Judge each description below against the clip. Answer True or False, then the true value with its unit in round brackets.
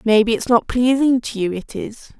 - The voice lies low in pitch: False (230 Hz)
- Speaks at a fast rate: True (220 wpm)